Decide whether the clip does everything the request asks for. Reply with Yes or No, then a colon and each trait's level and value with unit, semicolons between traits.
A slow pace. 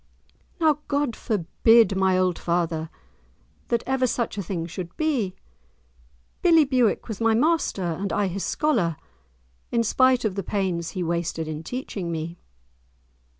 No: average, 145 wpm